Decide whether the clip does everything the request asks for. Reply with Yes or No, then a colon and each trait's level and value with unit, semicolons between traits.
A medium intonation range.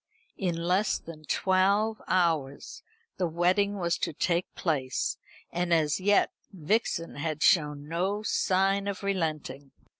Yes: average, 3.8 semitones